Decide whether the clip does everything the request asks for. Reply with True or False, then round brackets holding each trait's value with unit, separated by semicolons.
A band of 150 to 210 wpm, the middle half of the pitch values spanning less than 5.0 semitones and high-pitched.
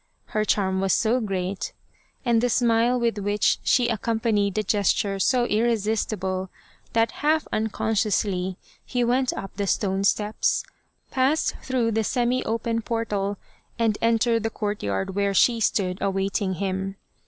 False (140 wpm; 3.0 semitones; 215 Hz)